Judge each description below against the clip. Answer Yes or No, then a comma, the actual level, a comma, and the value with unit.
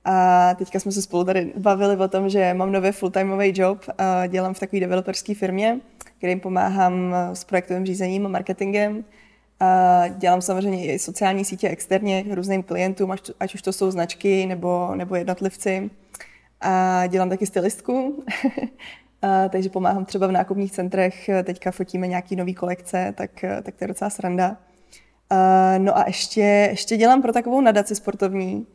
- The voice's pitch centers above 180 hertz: Yes, high, 190 Hz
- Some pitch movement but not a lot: No, narrow, 1.4 semitones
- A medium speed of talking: Yes, average, 155 wpm